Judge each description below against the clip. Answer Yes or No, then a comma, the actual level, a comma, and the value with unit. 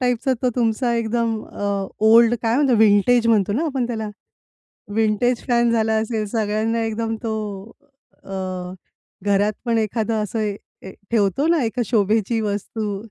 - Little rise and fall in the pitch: Yes, narrow, 1.9 semitones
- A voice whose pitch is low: No, high, 225 Hz